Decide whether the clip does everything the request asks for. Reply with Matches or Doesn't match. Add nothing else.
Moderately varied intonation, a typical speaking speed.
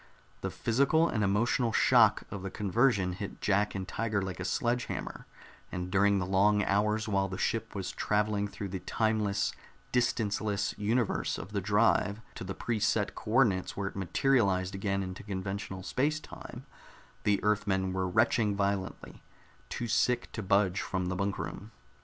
Doesn't match